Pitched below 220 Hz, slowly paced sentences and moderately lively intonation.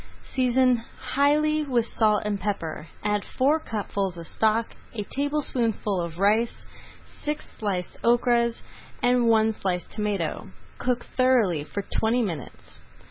No: high, 225 Hz; slow, 125 wpm; average, 3.9 semitones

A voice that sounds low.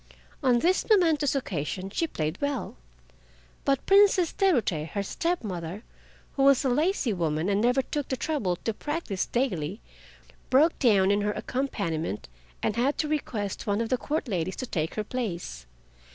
No: high, 235 Hz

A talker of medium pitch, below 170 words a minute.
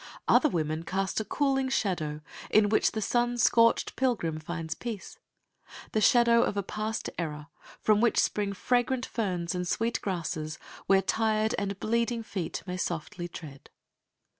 No: high, 200 Hz; average, 150 wpm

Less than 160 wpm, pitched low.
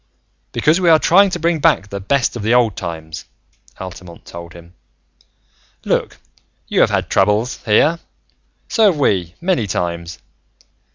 Yes: average, 150 wpm; low, 105 Hz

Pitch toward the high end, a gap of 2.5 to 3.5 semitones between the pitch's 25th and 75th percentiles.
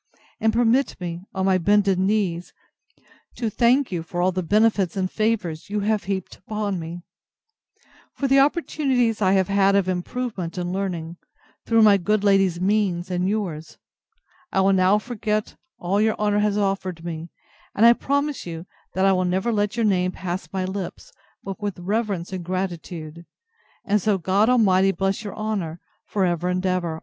Yes: high, 195 Hz; average, 2.9 semitones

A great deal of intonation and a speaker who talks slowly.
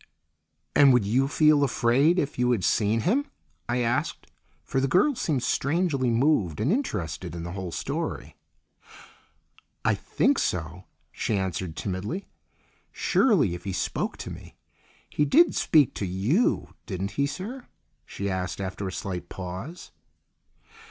No: wide, 8.3 semitones; average, 145 wpm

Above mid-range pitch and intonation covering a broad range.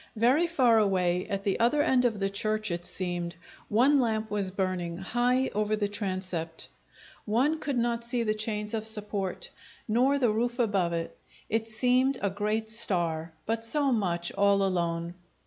No: high, 215 Hz; average, 4.0 semitones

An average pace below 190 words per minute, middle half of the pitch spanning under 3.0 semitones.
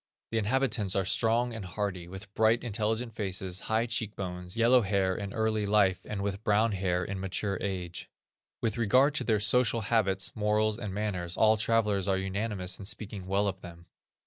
Yes: average, 180 wpm; narrow, 2.6 semitones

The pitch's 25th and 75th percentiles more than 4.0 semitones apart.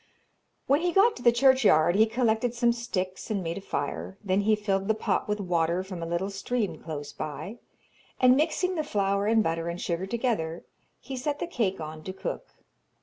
Yes: wide, 5.4 semitones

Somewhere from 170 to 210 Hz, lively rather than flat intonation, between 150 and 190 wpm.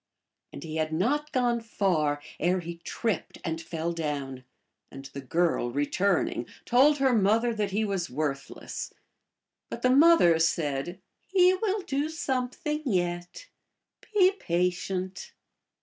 No: medium, 185 Hz; wide, 8.0 semitones; slow, 135 wpm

